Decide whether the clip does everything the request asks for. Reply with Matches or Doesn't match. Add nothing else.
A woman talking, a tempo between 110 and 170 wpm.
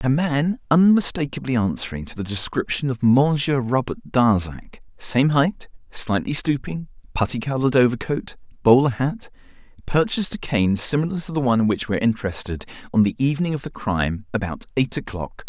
Doesn't match